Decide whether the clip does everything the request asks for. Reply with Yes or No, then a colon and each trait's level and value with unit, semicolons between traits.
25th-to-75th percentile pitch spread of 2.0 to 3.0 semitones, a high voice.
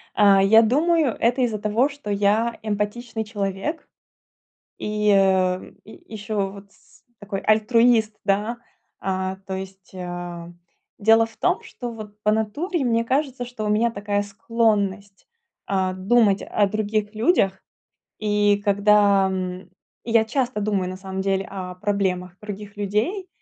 Yes: average, 2.7 semitones; high, 210 Hz